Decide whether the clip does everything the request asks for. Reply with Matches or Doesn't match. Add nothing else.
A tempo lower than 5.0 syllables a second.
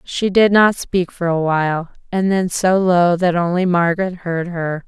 Matches